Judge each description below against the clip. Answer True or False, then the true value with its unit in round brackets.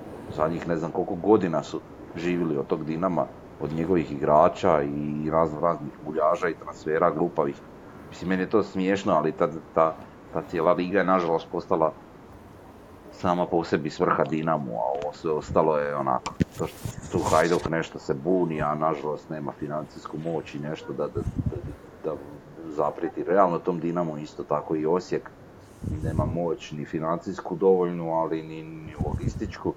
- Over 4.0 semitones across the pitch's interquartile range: False (2.4 semitones)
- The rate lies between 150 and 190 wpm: True (160 wpm)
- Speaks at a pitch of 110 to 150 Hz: False (80 Hz)